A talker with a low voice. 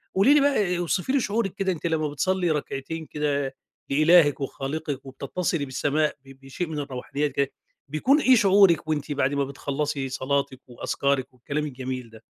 No: medium, 150 Hz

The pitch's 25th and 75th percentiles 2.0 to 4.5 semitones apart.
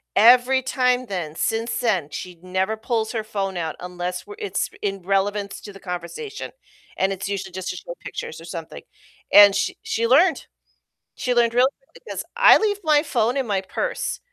No: average, 5.2 semitones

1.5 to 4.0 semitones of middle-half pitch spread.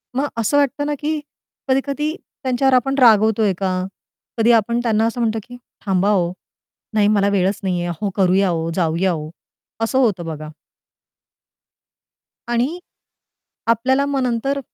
No: wide, 5.6 semitones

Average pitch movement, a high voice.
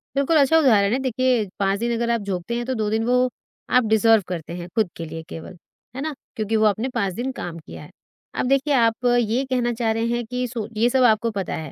Yes: average, 3.7 semitones; high, 230 Hz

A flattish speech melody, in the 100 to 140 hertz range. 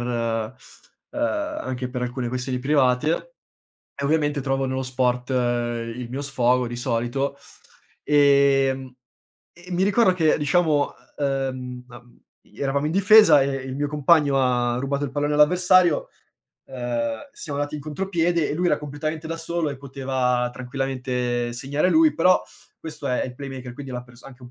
No: average, 3.3 semitones; low, 135 Hz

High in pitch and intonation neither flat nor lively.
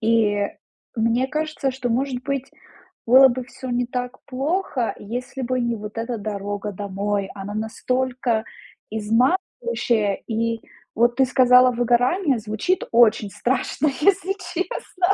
Yes: high, 245 Hz; average, 3.1 semitones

